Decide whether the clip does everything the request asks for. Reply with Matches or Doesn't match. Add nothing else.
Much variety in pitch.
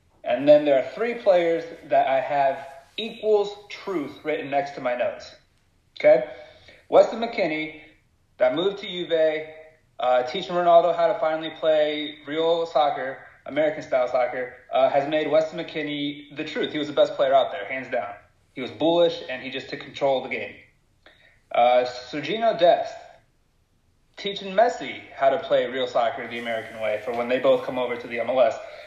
Matches